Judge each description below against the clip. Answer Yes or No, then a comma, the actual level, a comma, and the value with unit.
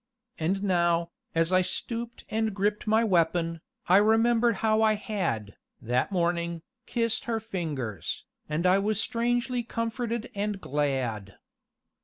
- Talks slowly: Yes, slow, 130 wpm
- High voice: Yes, high, 195 Hz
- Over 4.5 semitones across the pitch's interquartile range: Yes, average, 5.0 semitones